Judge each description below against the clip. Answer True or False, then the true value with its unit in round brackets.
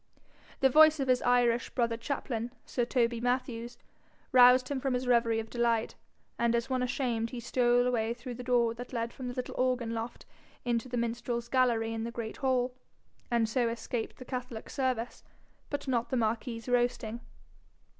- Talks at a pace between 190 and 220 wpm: False (175 wpm)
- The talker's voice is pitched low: False (240 Hz)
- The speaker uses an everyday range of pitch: False (1.5 semitones)